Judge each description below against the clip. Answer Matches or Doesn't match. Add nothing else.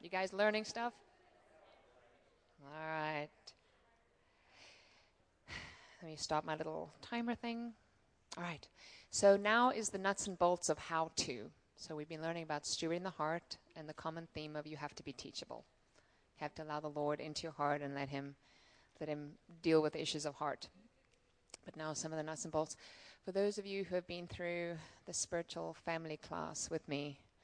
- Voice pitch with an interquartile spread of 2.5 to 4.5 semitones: Matches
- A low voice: Doesn't match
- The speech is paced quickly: Doesn't match